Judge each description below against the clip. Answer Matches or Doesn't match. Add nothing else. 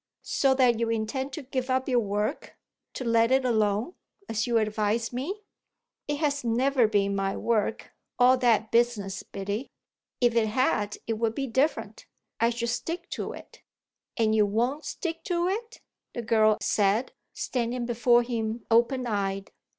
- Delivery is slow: Doesn't match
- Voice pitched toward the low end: Doesn't match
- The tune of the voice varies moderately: Matches